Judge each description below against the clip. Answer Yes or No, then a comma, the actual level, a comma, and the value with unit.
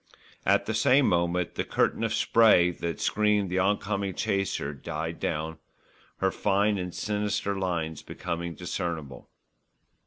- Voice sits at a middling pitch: No, very low, 90 Hz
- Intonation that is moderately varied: Yes, average, 3.5 semitones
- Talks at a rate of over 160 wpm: No, slow, 135 wpm